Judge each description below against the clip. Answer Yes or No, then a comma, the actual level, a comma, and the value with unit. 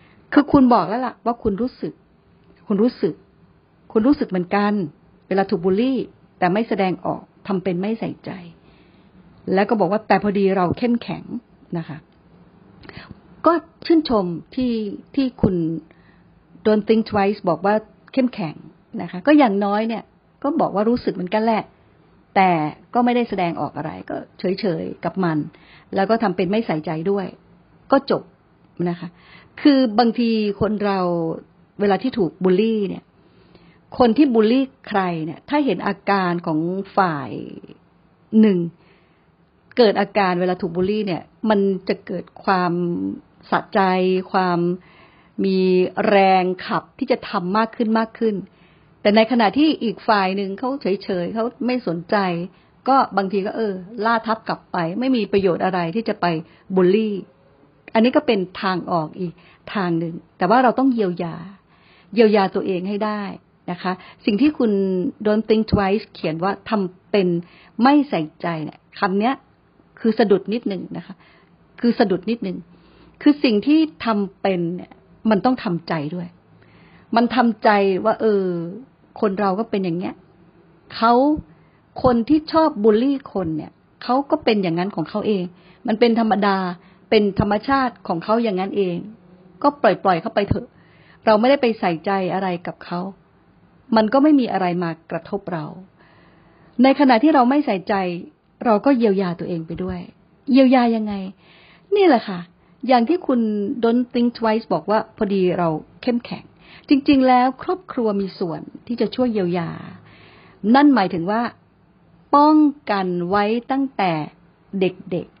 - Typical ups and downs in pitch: Yes, average, 4.4 semitones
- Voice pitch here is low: No, high, 200 Hz